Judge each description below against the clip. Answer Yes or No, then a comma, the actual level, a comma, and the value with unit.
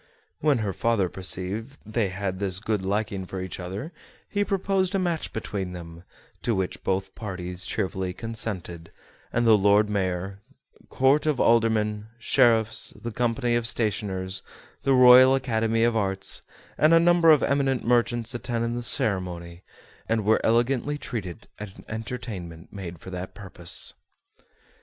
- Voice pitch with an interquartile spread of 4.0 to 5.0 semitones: Yes, average, 4.3 semitones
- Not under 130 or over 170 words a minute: Yes, average, 145 wpm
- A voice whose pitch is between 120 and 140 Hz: No, low, 110 Hz